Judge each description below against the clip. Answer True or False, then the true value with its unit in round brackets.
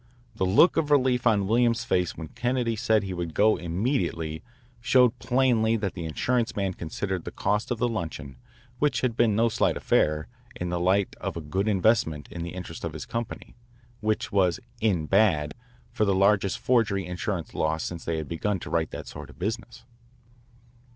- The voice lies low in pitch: True (100 Hz)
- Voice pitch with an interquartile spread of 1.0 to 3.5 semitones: False (5.1 semitones)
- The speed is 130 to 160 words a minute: False (185 wpm)